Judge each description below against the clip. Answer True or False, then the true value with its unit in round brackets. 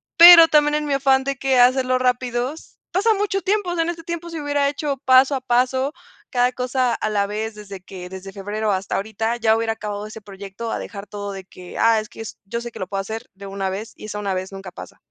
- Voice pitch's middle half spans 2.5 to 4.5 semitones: False (5.3 semitones)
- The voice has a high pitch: True (235 Hz)